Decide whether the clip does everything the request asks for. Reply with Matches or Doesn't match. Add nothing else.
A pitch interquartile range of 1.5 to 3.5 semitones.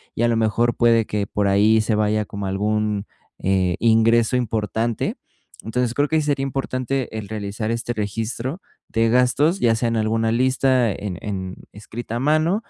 Matches